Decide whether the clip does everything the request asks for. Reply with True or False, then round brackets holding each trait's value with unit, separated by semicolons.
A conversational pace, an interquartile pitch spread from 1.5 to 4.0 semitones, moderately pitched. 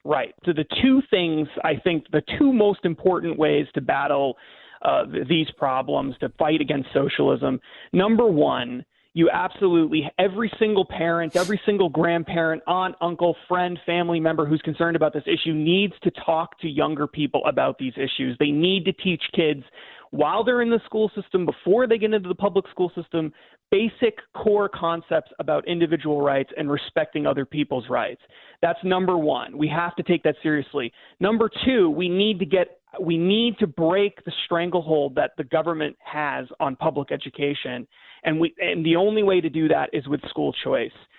True (175 wpm; 3.6 semitones; 170 Hz)